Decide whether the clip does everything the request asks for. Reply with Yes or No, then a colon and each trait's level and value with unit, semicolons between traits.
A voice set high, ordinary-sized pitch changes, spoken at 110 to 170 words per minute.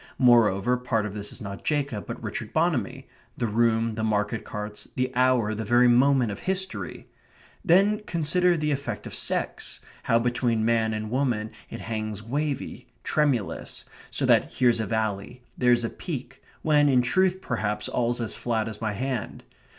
No: low, 120 Hz; average, 3.9 semitones; average, 165 wpm